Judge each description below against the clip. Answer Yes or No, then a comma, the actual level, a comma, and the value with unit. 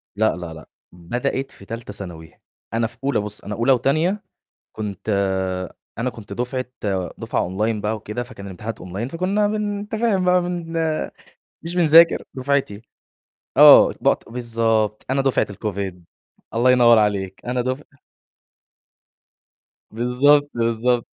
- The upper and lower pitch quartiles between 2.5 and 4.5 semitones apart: No, wide, 5.4 semitones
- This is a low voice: Yes, low, 120 Hz